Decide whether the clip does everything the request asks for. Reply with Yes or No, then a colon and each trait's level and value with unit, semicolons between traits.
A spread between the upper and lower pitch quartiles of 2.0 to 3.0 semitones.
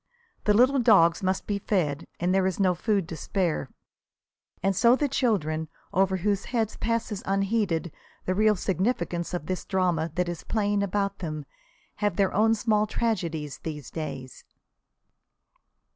No: average, 3.8 semitones